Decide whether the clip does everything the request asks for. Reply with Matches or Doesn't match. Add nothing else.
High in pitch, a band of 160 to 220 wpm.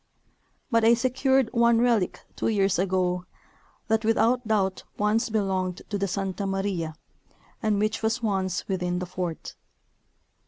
Doesn't match